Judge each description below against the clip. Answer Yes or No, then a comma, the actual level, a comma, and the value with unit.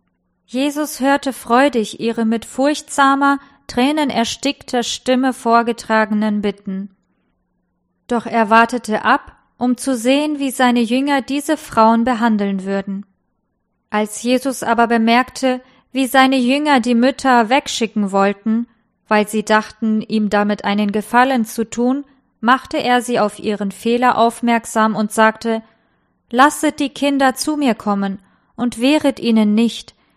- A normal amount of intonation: Yes, average, 3.4 semitones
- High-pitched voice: Yes, high, 235 Hz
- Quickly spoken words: No, slow, 125 wpm